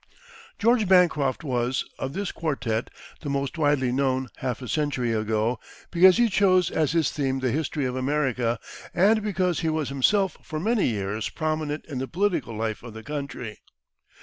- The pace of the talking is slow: No, average, 170 wpm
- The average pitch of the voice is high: No, medium, 140 Hz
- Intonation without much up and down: No, wide, 5.4 semitones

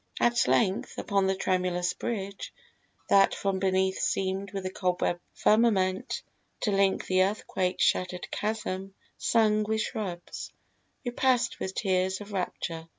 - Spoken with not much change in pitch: Yes, narrow, 2.2 semitones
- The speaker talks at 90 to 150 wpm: Yes, slow, 135 wpm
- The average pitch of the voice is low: No, high, 195 Hz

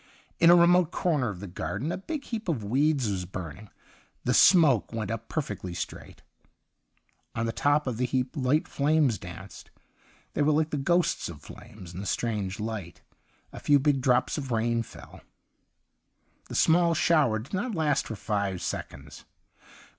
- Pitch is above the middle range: No, low, 125 Hz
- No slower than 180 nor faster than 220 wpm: No, average, 170 wpm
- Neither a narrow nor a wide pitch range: No, wide, 6.8 semitones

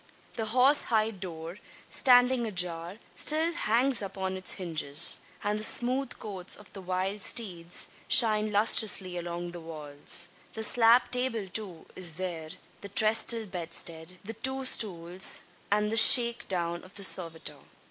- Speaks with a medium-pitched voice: No, high, 200 Hz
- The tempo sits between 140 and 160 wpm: Yes, average, 145 wpm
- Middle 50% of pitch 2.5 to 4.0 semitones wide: No, average, 4.5 semitones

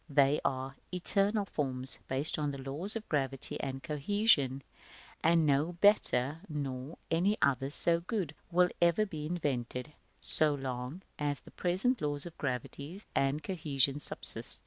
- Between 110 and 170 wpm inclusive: Yes, average, 140 wpm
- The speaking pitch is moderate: Yes, medium, 150 Hz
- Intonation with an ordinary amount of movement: Yes, average, 4.4 semitones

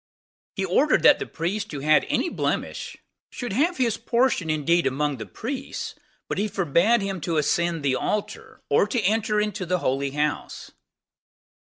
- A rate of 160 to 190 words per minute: Yes, average, 165 wpm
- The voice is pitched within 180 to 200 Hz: Yes, medium, 185 Hz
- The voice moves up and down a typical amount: No, wide, 6.5 semitones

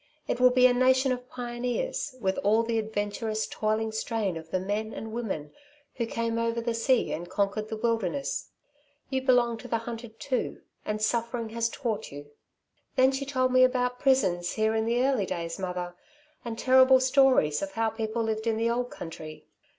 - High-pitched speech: Yes, high, 230 Hz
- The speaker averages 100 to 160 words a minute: No, average, 185 wpm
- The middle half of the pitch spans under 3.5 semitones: Yes, average, 2.8 semitones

